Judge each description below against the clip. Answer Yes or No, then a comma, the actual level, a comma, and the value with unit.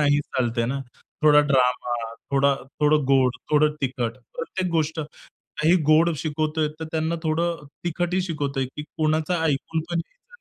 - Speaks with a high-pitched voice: No, medium, 155 Hz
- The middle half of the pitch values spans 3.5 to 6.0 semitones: No, average, 3.0 semitones